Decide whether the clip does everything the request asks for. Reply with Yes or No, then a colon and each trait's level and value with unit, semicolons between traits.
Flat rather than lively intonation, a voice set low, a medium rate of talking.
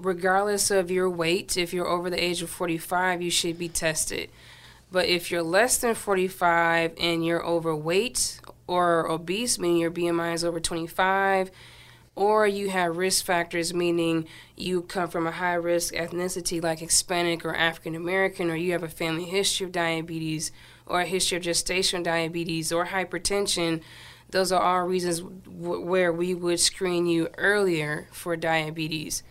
No: narrow, 1.7 semitones; medium, 175 Hz; average, 160 wpm